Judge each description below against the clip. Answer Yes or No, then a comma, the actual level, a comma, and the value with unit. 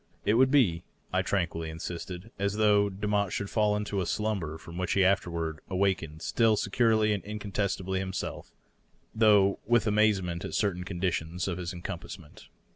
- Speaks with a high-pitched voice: No, low, 100 Hz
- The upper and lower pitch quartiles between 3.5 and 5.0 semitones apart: No, average, 3.1 semitones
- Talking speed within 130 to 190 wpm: Yes, average, 155 wpm